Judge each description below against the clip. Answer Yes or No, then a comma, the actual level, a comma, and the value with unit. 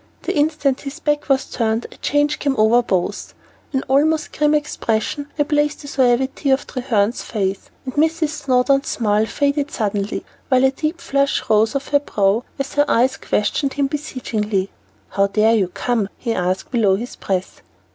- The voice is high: Yes, very high, 265 Hz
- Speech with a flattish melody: No, average, 5.1 semitones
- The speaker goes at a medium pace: Yes, average, 165 wpm